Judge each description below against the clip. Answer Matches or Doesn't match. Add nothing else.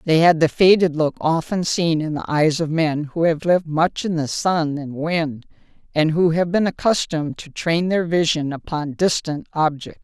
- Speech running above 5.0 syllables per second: Doesn't match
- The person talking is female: Matches